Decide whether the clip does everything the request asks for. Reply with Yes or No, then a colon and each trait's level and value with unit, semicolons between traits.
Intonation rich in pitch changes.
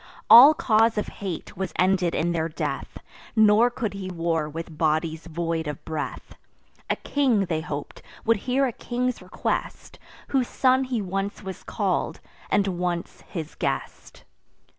Yes: wide, 5.7 semitones